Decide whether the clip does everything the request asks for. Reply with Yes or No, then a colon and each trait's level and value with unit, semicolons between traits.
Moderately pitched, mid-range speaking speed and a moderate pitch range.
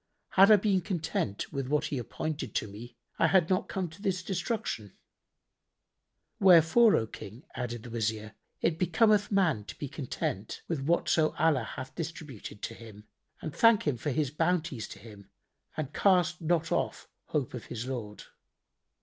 No: medium, 150 Hz; average, 160 wpm; wide, 7.3 semitones